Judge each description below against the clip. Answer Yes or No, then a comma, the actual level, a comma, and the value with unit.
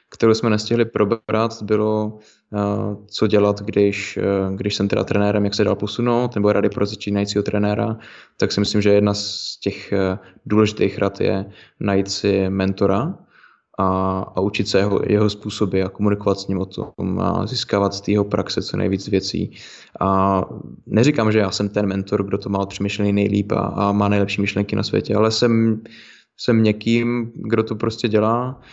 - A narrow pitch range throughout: Yes, narrow, 1.5 semitones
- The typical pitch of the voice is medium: No, low, 105 Hz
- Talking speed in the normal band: No, fast, 175 wpm